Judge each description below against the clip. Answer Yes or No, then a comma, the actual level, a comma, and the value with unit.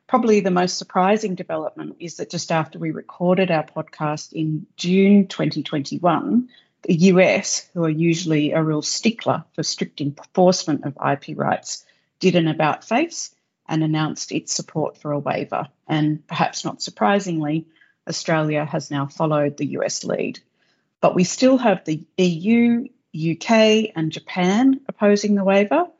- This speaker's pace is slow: No, average, 150 wpm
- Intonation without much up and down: No, average, 4.3 semitones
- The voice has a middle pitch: Yes, medium, 175 Hz